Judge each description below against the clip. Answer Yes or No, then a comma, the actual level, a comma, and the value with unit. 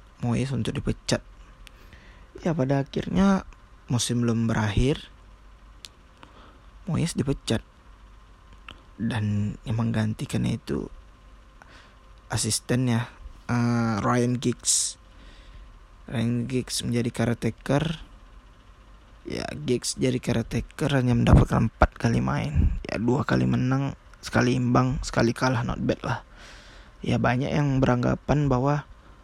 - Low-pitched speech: Yes, low, 115 Hz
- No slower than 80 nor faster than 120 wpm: Yes, average, 100 wpm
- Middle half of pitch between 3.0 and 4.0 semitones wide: Yes, average, 3.7 semitones